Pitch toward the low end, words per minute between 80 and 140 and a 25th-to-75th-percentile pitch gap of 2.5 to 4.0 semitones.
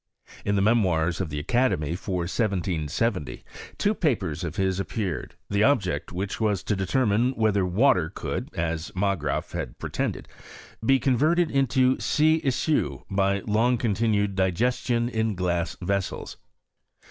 No: low, 100 Hz; slow, 135 wpm; average, 5.2 semitones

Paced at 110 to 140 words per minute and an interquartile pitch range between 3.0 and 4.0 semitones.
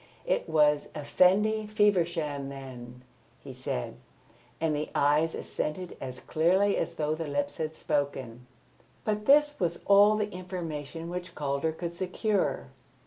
No: slow, 135 wpm; average, 4.7 semitones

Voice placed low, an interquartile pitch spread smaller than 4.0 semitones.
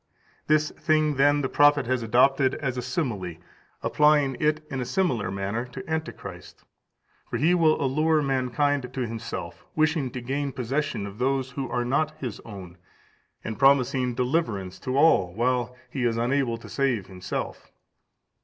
Yes: low, 130 Hz; average, 3.6 semitones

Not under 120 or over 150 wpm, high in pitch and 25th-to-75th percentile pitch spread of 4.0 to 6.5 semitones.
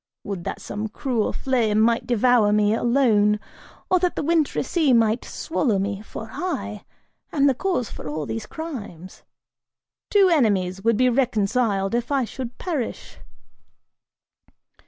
Yes: average, 140 wpm; high, 230 Hz; average, 4.6 semitones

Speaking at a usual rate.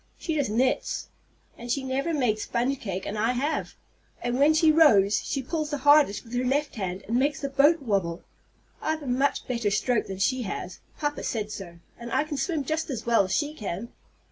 No: fast, 210 wpm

